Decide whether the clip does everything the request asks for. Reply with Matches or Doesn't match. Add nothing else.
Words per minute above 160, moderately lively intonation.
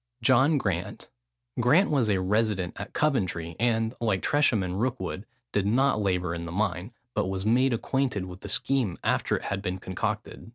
Matches